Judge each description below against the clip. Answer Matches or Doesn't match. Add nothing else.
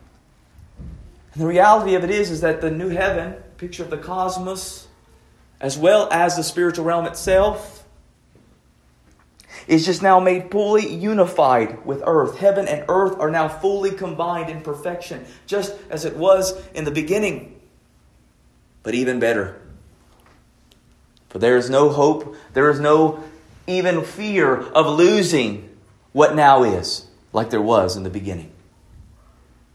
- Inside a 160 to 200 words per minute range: Doesn't match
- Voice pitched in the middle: Matches